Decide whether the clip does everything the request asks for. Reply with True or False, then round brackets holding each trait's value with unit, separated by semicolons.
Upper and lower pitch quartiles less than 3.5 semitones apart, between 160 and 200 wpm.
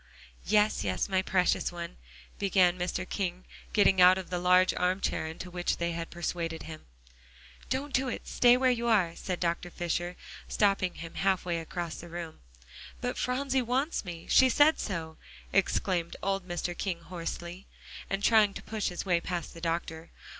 True (2.8 semitones; 175 wpm)